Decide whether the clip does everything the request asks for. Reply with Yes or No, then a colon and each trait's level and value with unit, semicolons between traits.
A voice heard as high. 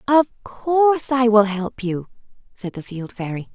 Yes: high, 230 Hz